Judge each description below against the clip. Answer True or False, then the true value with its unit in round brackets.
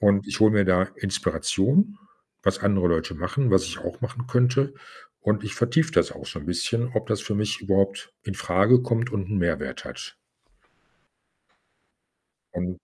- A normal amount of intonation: True (4.3 semitones)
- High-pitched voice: False (105 Hz)